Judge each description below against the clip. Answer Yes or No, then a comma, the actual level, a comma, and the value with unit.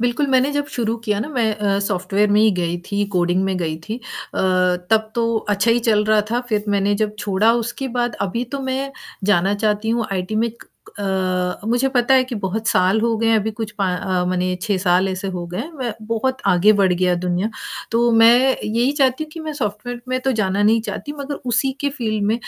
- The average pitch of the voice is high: Yes, high, 215 Hz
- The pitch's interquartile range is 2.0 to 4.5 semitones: Yes, average, 3.9 semitones